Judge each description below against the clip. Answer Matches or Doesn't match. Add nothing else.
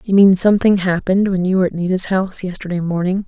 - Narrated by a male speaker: Doesn't match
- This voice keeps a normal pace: Doesn't match